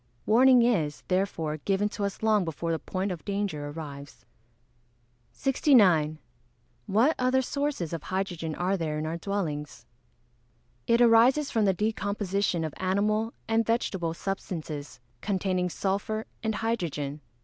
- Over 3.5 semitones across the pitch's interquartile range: Yes, average, 5.3 semitones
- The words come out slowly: Yes, slow, 130 wpm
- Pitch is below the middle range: No, high, 195 Hz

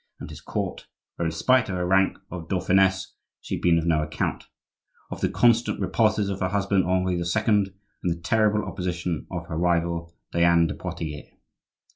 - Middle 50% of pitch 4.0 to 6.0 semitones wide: No, average, 2.8 semitones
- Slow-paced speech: No, average, 170 wpm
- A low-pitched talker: Yes, very low, 90 Hz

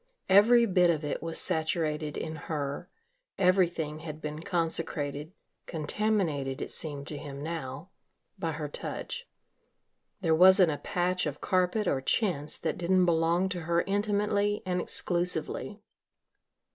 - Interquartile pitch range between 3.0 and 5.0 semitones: Yes, average, 3.5 semitones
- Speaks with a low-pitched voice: No, medium, 170 Hz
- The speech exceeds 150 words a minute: No, slow, 135 wpm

